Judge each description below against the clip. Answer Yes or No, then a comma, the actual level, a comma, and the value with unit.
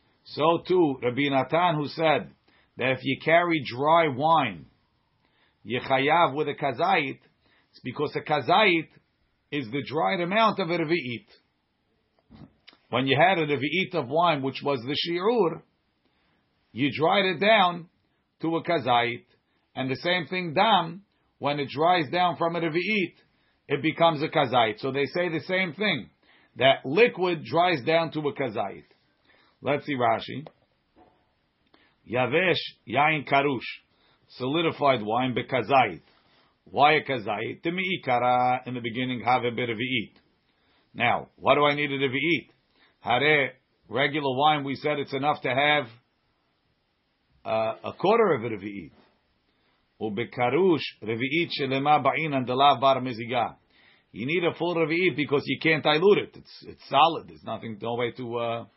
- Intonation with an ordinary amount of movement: Yes, average, 4.3 semitones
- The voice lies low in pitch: No, medium, 145 Hz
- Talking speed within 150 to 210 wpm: No, average, 140 wpm